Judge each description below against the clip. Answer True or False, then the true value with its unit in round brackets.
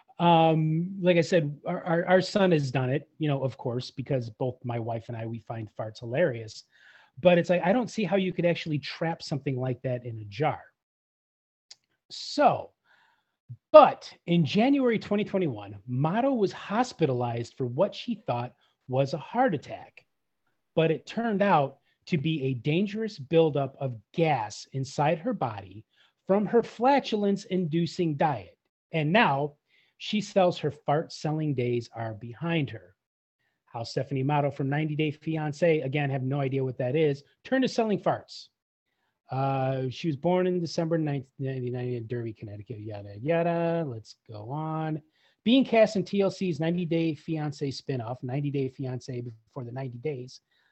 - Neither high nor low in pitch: True (150 Hz)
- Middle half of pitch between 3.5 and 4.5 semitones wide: False (5.5 semitones)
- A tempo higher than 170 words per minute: False (160 wpm)